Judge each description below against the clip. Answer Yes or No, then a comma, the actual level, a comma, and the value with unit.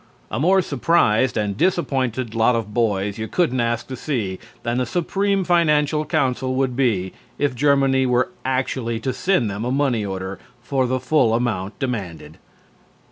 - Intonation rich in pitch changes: No, average, 4.1 semitones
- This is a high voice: No, low, 125 Hz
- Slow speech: No, average, 160 wpm